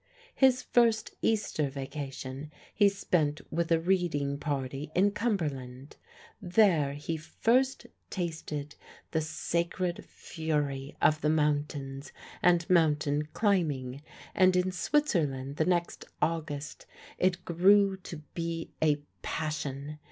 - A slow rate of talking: Yes, slow, 110 wpm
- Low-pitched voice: No, medium, 160 Hz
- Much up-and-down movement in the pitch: No, average, 3.9 semitones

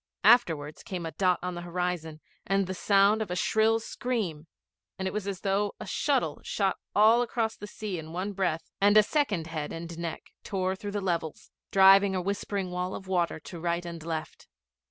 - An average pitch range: Yes, average, 3.3 semitones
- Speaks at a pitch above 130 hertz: Yes, high, 190 Hz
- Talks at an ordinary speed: Yes, average, 195 wpm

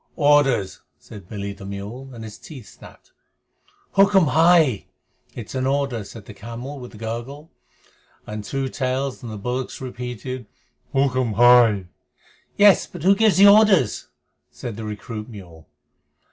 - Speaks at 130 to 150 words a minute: Yes, average, 145 wpm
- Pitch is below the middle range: Yes, low, 125 Hz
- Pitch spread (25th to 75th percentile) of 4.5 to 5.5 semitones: Yes, average, 4.8 semitones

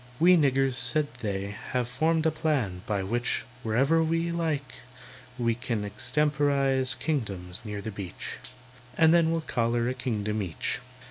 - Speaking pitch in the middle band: No, low, 130 Hz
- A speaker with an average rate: Yes, average, 145 wpm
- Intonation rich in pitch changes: Yes, wide, 6.4 semitones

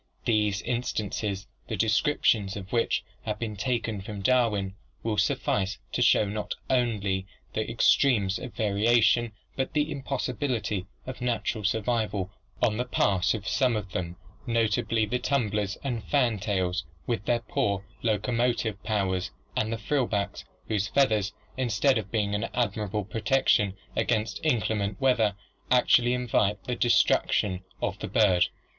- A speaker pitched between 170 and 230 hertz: No, low, 110 Hz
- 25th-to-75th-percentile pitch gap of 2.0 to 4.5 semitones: Yes, average, 3.1 semitones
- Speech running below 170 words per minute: Yes, average, 140 wpm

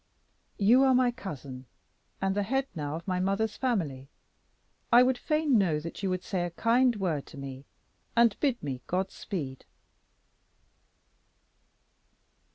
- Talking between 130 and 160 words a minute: Yes, average, 145 wpm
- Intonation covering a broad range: Yes, wide, 8.0 semitones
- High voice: Yes, high, 195 Hz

